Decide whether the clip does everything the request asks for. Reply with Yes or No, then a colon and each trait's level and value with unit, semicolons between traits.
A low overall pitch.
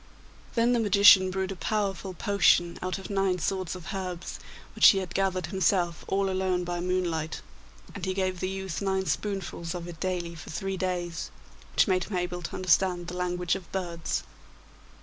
No: medium, 185 Hz